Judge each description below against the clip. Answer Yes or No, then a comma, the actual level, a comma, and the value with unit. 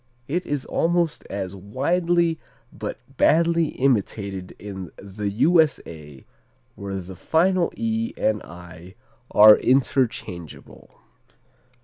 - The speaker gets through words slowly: Yes, slow, 95 wpm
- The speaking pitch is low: Yes, low, 110 Hz